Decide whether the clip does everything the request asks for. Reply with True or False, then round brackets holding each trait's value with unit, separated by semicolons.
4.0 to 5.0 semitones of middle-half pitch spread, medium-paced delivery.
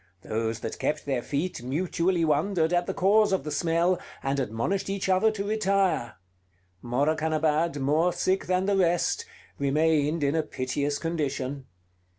True (4.7 semitones; 150 wpm)